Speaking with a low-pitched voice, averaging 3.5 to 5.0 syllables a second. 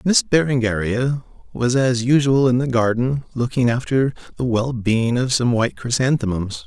Yes: low, 125 Hz; 4.7 syllables/s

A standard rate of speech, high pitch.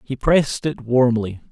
No: average, 160 wpm; low, 125 Hz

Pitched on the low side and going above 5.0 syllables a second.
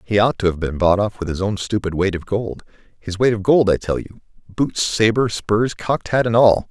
Yes: low, 105 Hz; 5.2 syllables/s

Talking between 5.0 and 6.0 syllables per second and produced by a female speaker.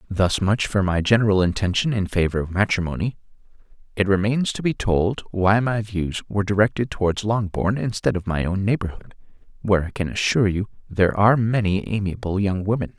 No: 5.7 syllables/s; male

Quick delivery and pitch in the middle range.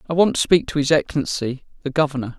Yes: fast, 225 wpm; medium, 150 Hz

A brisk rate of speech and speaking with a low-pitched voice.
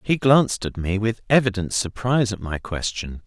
No: average, 185 wpm; low, 105 Hz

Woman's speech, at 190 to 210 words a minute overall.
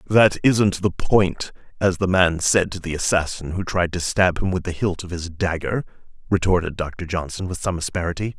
No: male; average, 200 wpm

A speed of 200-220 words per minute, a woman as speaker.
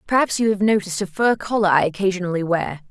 Yes: fast, 205 wpm; female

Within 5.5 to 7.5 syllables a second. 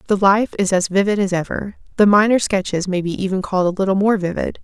Yes: 6.3 syllables/s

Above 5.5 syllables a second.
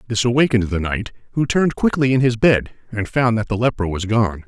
Yes: 5.9 syllables/s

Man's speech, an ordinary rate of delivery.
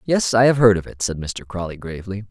No: male; fast, 260 wpm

